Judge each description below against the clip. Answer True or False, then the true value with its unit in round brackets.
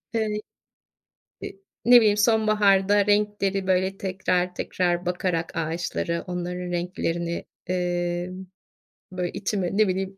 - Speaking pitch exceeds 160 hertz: True (185 Hz)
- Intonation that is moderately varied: False (2.2 semitones)